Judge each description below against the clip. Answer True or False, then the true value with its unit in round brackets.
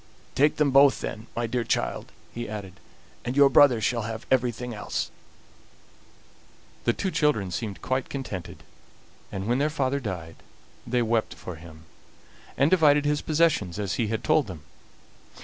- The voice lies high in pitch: False (120 Hz)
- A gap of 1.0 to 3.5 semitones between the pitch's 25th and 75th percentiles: False (5.2 semitones)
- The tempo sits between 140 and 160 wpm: True (155 wpm)